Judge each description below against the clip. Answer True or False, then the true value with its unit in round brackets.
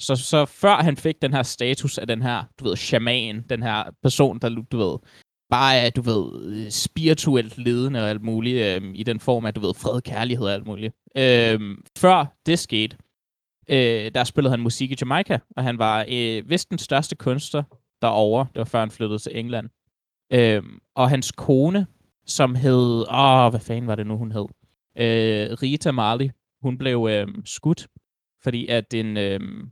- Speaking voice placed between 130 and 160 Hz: False (120 Hz)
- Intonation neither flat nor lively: True (3.4 semitones)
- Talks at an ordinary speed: True (185 wpm)